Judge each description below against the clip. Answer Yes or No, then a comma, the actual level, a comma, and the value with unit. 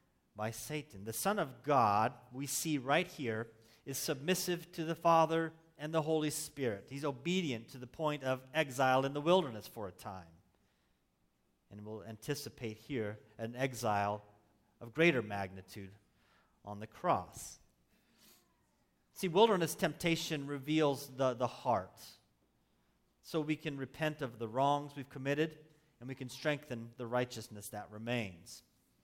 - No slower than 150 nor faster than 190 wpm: No, average, 140 wpm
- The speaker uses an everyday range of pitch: No, wide, 6.7 semitones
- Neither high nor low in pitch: No, low, 125 Hz